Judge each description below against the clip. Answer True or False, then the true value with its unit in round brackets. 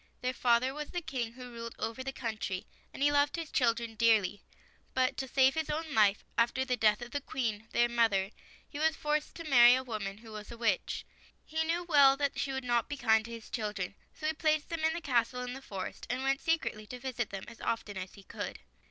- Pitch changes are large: False (4.2 semitones)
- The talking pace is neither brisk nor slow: False (240 wpm)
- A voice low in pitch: False (250 Hz)